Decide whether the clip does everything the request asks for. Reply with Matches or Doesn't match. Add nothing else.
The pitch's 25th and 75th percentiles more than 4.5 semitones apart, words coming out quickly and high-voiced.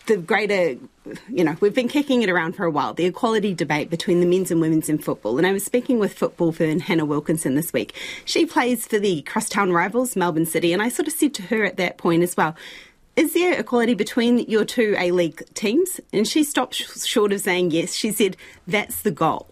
Matches